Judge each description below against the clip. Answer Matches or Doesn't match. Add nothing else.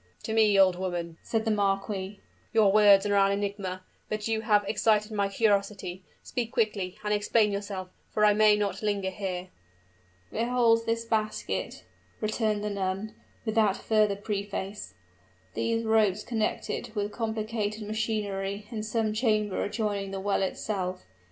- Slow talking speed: Doesn't match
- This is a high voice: Matches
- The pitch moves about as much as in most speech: Doesn't match